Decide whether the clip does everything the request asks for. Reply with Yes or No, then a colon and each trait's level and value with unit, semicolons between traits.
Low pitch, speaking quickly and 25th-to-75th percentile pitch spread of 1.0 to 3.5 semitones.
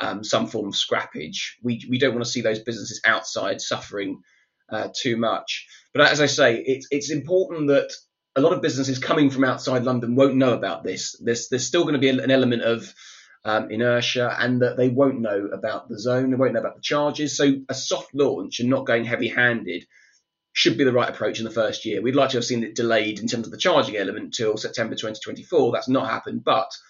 Yes: low, 125 Hz; fast, 225 wpm; narrow, 2.5 semitones